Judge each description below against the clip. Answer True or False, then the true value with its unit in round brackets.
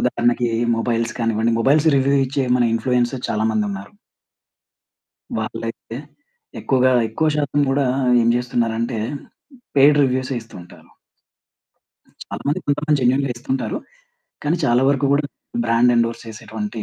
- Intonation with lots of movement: False (3.1 semitones)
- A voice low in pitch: True (125 Hz)